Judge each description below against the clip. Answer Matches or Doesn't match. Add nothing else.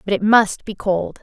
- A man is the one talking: Doesn't match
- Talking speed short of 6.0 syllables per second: Matches